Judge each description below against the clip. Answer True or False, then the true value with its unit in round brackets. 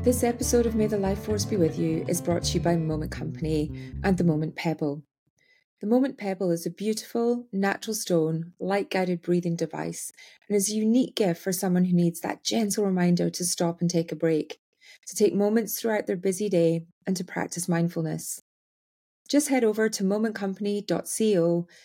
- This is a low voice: False (180 Hz)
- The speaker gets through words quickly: False (185 wpm)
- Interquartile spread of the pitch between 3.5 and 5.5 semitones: True (4.1 semitones)